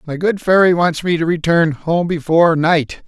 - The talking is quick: No, average, 195 wpm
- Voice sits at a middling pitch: Yes, medium, 165 Hz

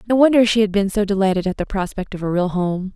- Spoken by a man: No, female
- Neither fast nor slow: No, fast, 285 wpm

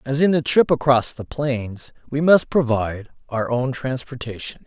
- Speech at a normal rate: Yes, average, 165 wpm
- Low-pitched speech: Yes, low, 130 Hz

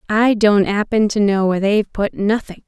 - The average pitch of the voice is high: Yes, high, 205 Hz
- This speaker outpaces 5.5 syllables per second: No, 5.2 syllables/s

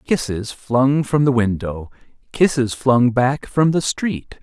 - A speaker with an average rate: Yes, average, 150 wpm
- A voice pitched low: Yes, low, 130 Hz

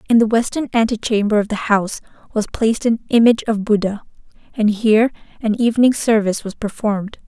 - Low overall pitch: No, high, 220 Hz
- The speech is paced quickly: No, average, 165 wpm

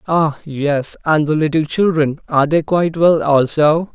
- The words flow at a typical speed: Yes, average, 165 wpm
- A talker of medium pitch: Yes, medium, 155 Hz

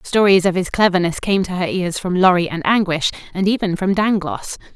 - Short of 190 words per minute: No, average, 200 wpm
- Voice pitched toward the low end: No, medium, 185 Hz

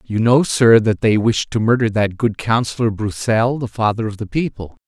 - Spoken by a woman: No, male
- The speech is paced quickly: Yes, fast, 210 wpm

